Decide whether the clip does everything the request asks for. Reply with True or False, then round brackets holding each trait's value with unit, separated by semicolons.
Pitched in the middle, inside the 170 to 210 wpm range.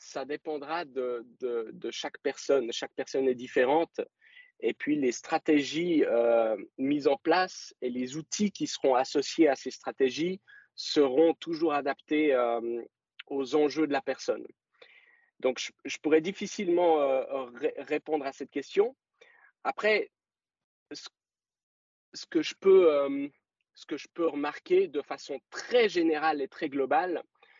False (160 Hz; 145 wpm)